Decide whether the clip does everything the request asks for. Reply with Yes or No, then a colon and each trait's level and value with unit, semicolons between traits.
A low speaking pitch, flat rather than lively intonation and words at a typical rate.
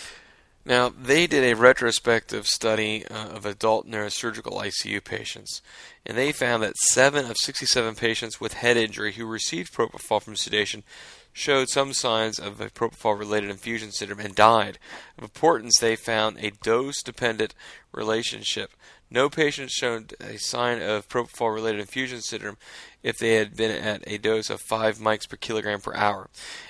Yes: low, 110 Hz; narrow, 2.1 semitones; average, 160 wpm